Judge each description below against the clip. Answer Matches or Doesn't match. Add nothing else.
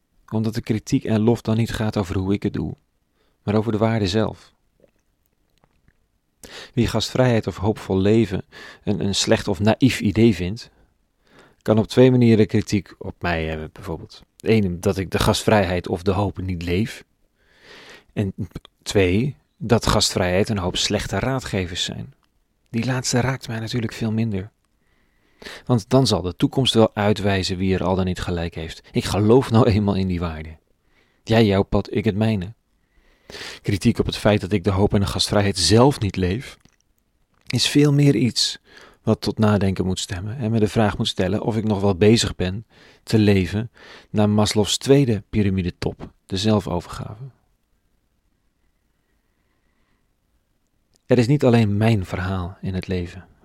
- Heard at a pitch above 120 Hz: Doesn't match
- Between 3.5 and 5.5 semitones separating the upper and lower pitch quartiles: Doesn't match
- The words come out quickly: Doesn't match